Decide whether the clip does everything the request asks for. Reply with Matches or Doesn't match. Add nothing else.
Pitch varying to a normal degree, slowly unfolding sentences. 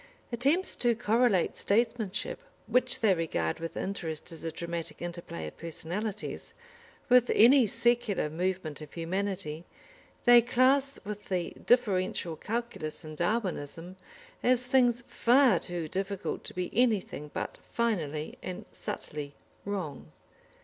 Doesn't match